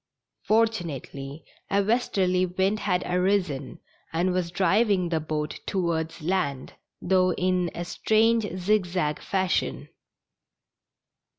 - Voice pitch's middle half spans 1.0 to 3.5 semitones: Yes, average, 2.8 semitones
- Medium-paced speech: No, slow, 105 wpm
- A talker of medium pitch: Yes, medium, 180 Hz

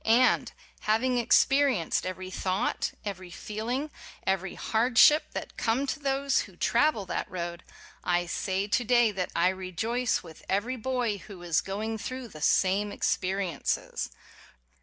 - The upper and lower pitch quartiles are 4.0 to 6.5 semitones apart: Yes, average, 4.9 semitones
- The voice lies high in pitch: Yes, high, 210 Hz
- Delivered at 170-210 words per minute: No, average, 145 wpm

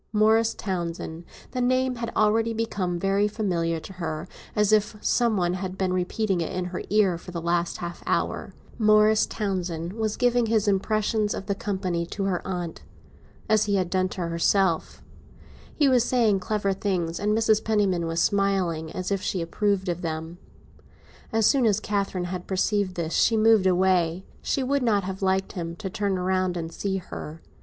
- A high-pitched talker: Yes, high, 195 Hz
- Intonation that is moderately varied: Yes, average, 3.3 semitones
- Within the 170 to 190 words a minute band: Yes, average, 175 wpm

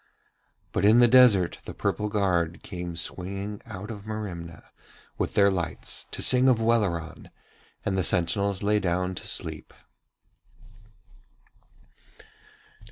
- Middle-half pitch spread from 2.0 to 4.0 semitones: Yes, average, 3.2 semitones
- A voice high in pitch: No, low, 100 Hz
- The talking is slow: Yes, slow, 120 wpm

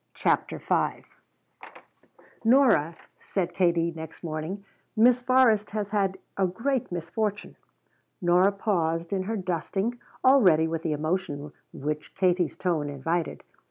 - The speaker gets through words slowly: Yes, slow, 125 wpm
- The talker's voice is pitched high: No, medium, 180 Hz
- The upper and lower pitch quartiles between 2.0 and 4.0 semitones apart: No, average, 4.4 semitones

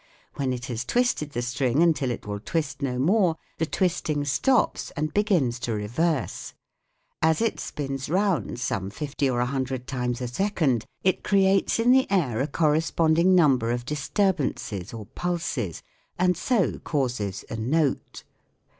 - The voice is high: No, medium, 145 Hz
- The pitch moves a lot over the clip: Yes, wide, 6.0 semitones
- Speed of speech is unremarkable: Yes, average, 170 wpm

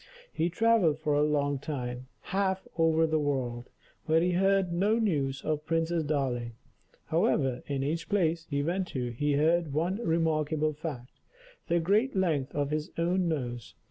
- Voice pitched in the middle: Yes, medium, 155 Hz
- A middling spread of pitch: Yes, average, 3.4 semitones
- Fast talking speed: No, average, 160 wpm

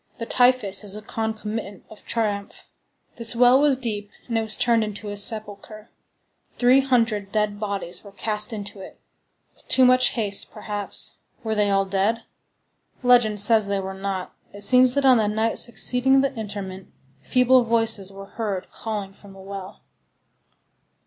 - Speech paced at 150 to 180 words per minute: Yes, average, 160 wpm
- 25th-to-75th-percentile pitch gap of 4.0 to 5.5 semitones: No, average, 2.8 semitones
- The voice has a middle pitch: No, high, 215 Hz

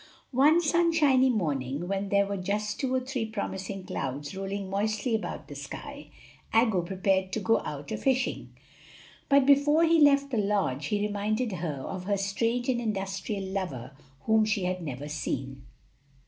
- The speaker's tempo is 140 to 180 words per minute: Yes, average, 160 wpm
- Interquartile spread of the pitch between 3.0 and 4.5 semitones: No, average, 5.1 semitones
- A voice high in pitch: Yes, high, 200 Hz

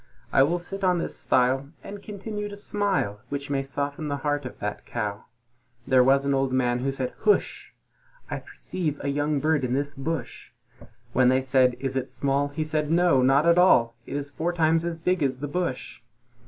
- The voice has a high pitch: No, medium, 140 Hz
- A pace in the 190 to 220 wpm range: Yes, average, 195 wpm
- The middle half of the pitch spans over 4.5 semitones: No, average, 4.0 semitones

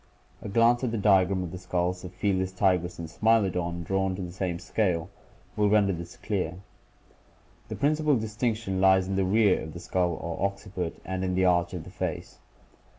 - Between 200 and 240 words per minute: Yes, fast, 205 wpm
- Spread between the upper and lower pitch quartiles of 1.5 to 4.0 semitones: Yes, narrow, 2.5 semitones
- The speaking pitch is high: No, very low, 95 Hz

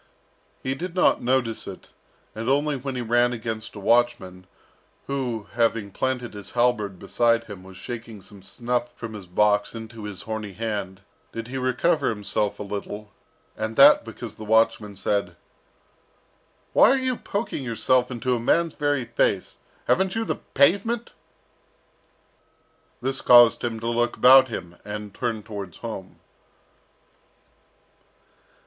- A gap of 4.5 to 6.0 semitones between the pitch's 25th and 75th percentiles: No, average, 3.7 semitones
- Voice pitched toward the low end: Yes, low, 115 Hz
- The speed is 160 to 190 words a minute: No, average, 140 wpm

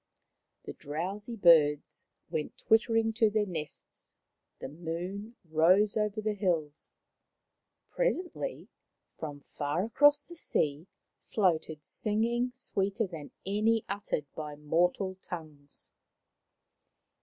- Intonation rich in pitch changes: Yes, wide, 5.8 semitones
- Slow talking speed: Yes, slow, 105 wpm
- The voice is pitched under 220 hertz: Yes, high, 190 Hz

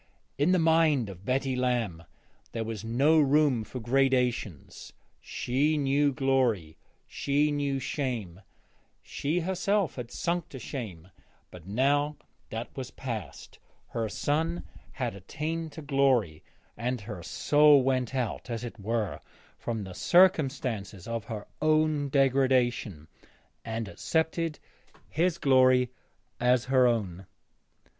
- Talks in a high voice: No, low, 130 Hz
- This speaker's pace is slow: Yes, slow, 120 wpm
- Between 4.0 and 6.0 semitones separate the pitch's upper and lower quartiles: Yes, average, 4.5 semitones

